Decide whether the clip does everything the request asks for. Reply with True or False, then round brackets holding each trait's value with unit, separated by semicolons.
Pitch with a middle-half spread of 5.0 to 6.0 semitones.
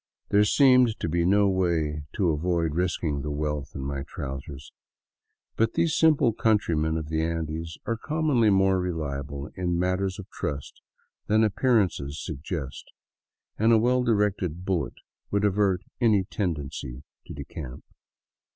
True (5.6 semitones)